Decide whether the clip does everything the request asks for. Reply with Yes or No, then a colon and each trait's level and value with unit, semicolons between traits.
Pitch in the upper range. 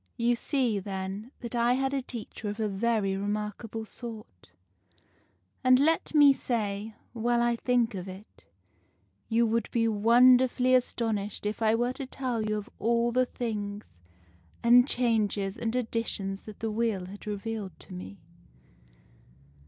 Yes: high, 225 Hz